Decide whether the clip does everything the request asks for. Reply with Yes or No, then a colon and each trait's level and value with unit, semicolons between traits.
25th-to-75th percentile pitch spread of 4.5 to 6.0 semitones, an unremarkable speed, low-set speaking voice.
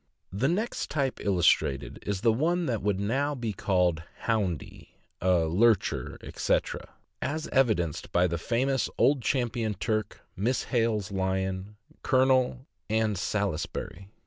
No: average, 5.3 semitones; slow, 125 wpm; low, 110 Hz